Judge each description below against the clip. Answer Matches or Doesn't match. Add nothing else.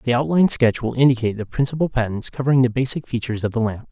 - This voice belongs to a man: Matches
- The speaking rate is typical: Doesn't match